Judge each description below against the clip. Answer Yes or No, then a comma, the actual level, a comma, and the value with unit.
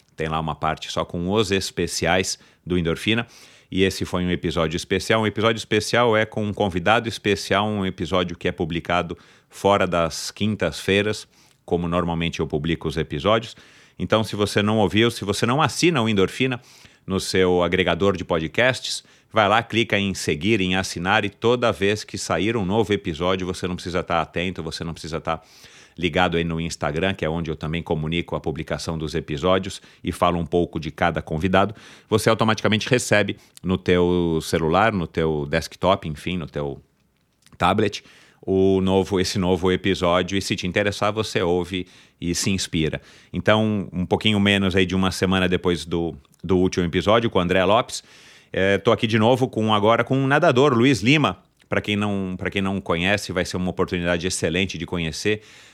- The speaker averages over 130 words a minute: Yes, average, 180 wpm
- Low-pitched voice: Yes, very low, 95 Hz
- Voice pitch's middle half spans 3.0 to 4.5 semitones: Yes, average, 3.3 semitones